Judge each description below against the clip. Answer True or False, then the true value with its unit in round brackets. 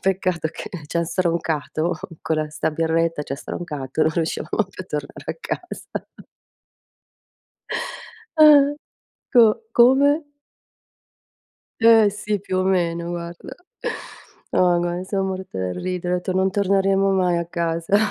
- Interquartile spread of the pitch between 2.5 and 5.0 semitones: True (2.9 semitones)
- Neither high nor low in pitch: True (180 Hz)